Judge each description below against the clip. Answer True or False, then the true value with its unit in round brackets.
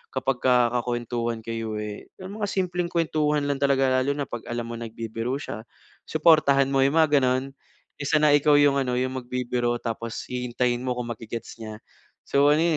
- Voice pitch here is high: False (130 Hz)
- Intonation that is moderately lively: True (3.4 semitones)